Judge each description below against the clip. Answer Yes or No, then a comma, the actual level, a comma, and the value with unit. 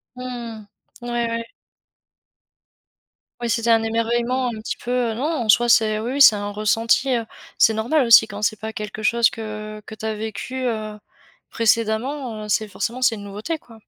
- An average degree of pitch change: No, narrow, 2.0 semitones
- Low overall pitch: No, high, 225 Hz